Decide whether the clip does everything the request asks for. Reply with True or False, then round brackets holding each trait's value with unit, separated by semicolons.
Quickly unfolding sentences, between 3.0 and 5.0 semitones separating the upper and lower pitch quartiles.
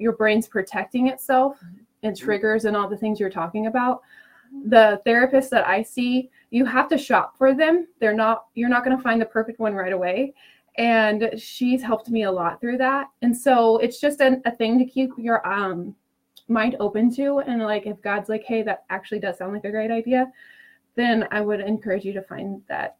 True (210 wpm; 3.4 semitones)